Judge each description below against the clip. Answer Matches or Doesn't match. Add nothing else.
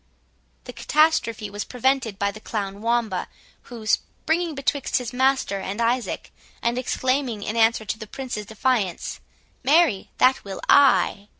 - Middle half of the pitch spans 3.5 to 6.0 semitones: Matches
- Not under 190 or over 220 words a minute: Doesn't match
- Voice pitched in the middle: Doesn't match